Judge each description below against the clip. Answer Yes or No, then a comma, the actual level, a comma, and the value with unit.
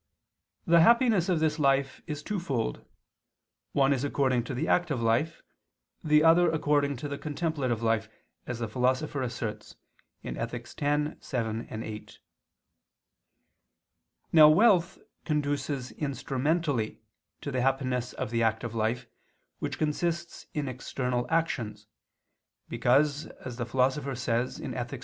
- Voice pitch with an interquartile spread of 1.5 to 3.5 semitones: No, average, 4.1 semitones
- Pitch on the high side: No, low, 135 Hz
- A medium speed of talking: No, slow, 120 wpm